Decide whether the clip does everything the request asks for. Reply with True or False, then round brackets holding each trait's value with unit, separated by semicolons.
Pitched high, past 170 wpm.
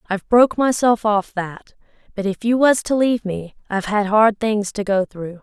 True (210 Hz; 200 wpm)